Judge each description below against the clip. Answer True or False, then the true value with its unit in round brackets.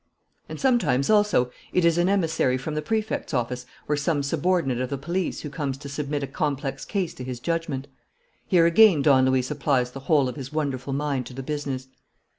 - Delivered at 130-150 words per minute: False (200 wpm)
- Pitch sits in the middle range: True (145 Hz)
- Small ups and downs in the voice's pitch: False (4.0 semitones)